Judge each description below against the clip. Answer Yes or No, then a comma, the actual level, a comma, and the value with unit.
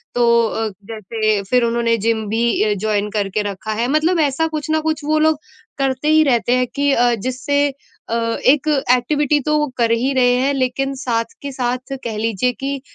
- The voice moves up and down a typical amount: Yes, average, 3.7 semitones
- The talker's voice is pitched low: No, very high, 250 Hz